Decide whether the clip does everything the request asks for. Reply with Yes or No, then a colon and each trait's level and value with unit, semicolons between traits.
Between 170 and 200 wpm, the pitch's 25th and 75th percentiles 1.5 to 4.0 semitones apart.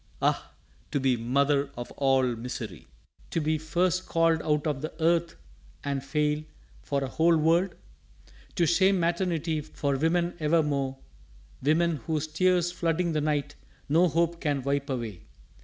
No: average, 145 wpm; average, 3.3 semitones